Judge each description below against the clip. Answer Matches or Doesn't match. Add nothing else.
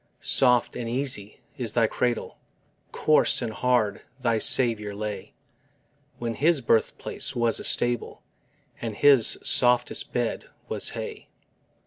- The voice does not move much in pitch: Matches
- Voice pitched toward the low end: Matches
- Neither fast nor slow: Doesn't match